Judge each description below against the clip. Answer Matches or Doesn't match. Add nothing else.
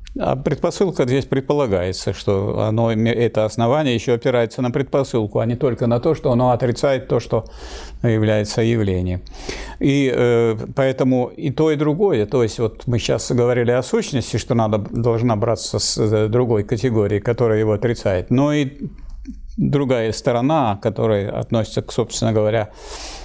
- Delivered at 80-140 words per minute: Doesn't match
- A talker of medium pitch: Doesn't match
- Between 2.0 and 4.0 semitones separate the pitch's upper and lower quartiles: Matches